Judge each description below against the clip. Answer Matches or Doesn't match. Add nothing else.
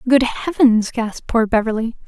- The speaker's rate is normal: Matches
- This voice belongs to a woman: Matches